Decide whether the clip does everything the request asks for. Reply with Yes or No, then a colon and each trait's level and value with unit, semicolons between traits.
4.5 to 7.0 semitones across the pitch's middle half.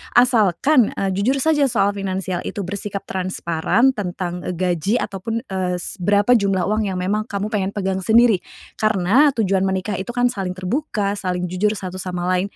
No: average, 2.8 semitones